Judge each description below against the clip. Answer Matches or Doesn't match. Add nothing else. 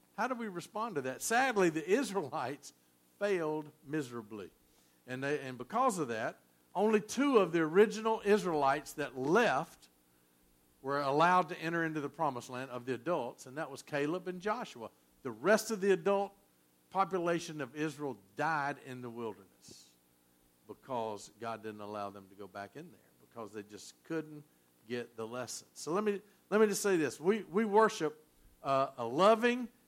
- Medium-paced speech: Matches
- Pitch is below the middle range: Doesn't match